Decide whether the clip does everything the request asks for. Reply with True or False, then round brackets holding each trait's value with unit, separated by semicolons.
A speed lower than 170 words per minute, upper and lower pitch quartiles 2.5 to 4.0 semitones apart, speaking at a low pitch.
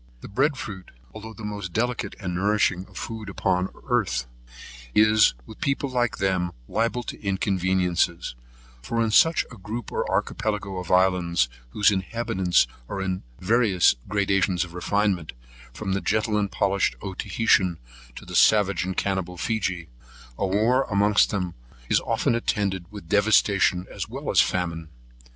True (150 wpm; 3.0 semitones; 100 Hz)